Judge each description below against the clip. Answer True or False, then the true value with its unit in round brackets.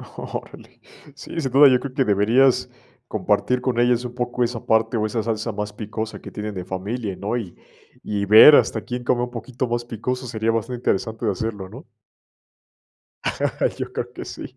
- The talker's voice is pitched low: True (115 Hz)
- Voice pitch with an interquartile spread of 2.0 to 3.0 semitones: True (2.7 semitones)